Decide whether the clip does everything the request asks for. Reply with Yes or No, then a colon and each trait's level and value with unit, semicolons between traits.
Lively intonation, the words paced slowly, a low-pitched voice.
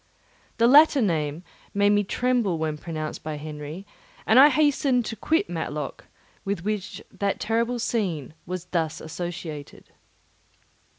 No: wide, 6.9 semitones; slow, 130 wpm; high, 195 Hz